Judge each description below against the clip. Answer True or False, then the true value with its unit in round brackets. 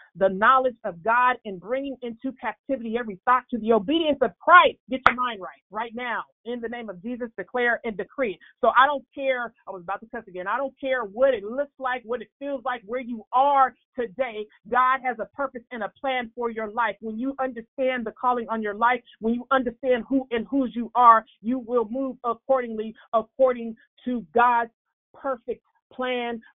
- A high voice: True (245 Hz)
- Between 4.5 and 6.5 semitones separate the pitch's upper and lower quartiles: False (2.5 semitones)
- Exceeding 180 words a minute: True (200 wpm)